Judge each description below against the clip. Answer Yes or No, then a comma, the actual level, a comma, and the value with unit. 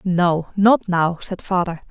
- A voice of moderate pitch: Yes, medium, 180 Hz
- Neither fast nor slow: Yes, average, 160 wpm